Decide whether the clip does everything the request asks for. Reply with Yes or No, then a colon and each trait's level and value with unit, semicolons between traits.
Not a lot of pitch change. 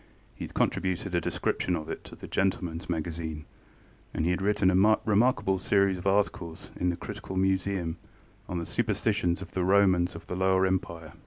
Yes: narrow, 2.3 semitones